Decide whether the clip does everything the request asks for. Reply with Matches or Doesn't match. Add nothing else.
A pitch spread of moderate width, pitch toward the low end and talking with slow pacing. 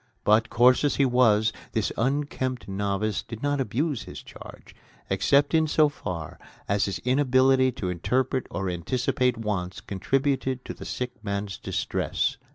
Doesn't match